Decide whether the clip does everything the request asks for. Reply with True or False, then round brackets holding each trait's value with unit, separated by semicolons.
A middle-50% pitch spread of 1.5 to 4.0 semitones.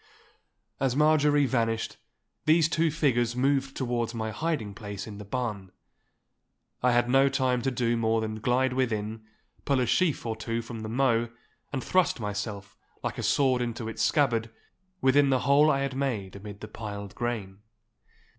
True (3.6 semitones)